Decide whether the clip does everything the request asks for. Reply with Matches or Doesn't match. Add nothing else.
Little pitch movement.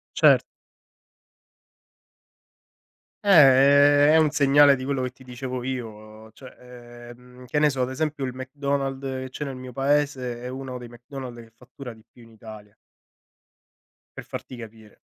Matches